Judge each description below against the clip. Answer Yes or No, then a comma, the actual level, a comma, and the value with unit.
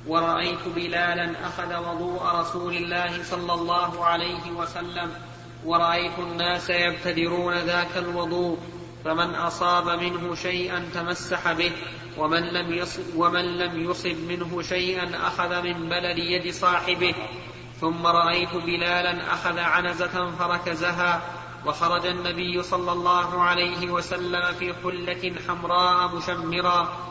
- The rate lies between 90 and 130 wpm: Yes, average, 110 wpm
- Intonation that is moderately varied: No, narrow, 0.5 semitones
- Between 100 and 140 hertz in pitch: No, medium, 175 Hz